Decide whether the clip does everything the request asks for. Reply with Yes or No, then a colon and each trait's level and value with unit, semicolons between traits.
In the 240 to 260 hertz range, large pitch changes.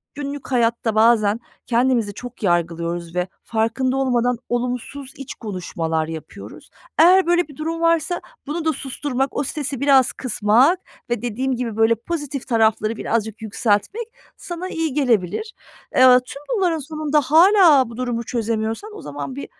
No: very high, 250 Hz; average, 5.0 semitones